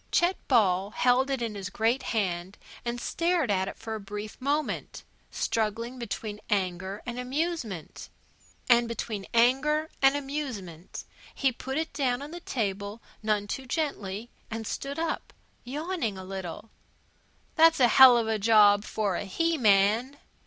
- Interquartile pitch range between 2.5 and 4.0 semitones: No, average, 5.0 semitones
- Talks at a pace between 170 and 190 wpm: No, average, 150 wpm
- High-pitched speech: Yes, high, 230 Hz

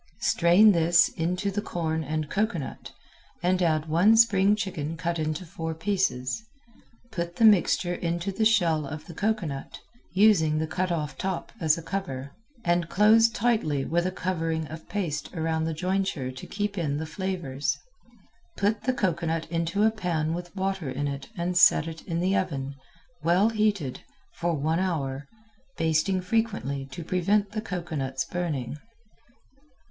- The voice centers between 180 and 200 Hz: No, medium, 170 Hz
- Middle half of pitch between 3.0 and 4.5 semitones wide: Yes, average, 3.7 semitones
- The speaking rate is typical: Yes, average, 155 wpm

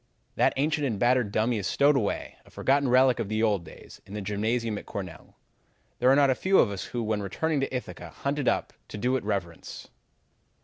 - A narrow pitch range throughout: No, average, 4.5 semitones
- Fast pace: Yes, fast, 220 wpm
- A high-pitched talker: No, low, 120 Hz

